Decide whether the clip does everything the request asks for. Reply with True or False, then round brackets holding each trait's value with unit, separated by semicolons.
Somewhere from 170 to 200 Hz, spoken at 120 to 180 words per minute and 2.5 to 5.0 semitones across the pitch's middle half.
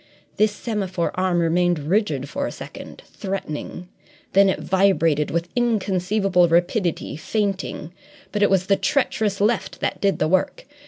True (190 Hz; 145 wpm; 3.2 semitones)